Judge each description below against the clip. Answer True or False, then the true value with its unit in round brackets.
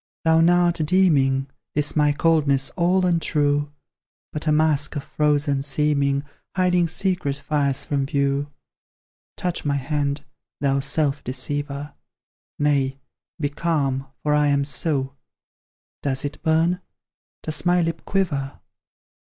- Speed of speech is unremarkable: False (125 wpm)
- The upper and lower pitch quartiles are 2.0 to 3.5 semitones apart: True (2.7 semitones)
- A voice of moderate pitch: True (145 Hz)